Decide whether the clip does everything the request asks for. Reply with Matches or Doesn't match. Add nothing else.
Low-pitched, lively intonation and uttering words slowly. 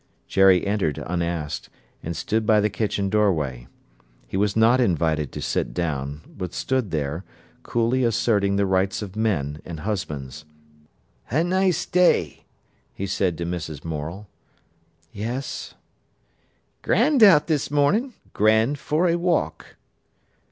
Matches